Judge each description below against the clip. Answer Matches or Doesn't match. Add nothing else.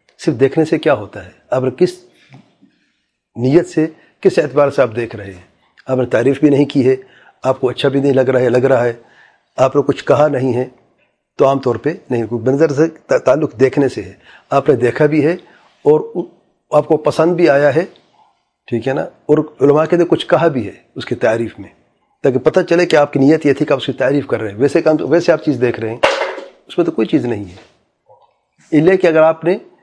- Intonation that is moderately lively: Matches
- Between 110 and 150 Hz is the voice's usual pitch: Matches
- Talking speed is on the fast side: Matches